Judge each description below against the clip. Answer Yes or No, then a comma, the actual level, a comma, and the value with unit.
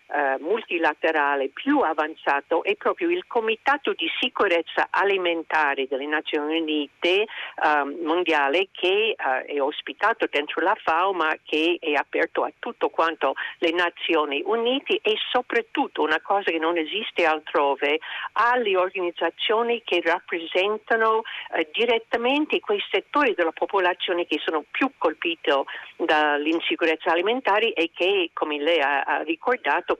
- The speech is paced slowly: No, average, 125 wpm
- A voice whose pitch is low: No, medium, 185 Hz